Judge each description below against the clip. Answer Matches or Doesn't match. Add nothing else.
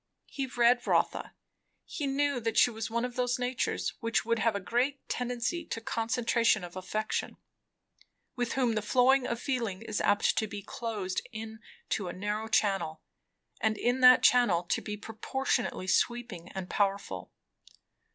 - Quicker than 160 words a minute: Doesn't match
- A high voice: Matches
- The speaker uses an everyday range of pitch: Matches